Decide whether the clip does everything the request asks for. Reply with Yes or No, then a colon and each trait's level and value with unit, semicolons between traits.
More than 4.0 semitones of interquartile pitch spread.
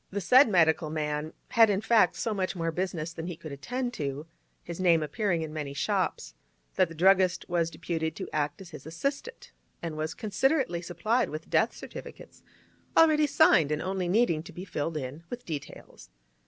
Yes: average, 4.4 semitones